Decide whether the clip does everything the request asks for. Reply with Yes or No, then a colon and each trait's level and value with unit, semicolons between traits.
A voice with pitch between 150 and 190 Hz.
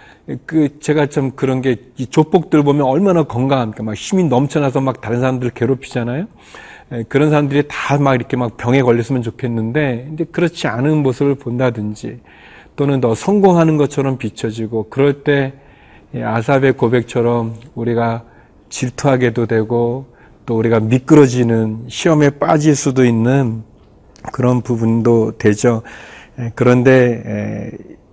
No: low, 125 Hz